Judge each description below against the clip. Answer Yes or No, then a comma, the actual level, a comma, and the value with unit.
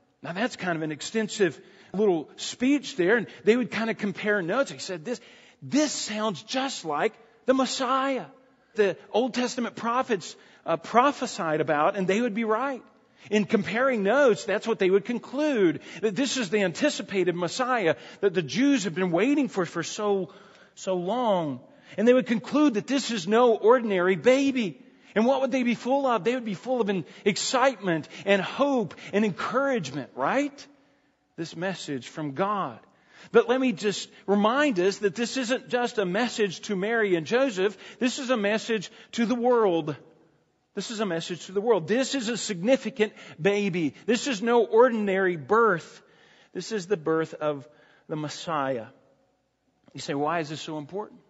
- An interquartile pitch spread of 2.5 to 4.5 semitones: No, average, 5.0 semitones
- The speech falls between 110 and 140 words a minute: No, average, 175 wpm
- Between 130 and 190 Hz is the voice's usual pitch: No, high, 215 Hz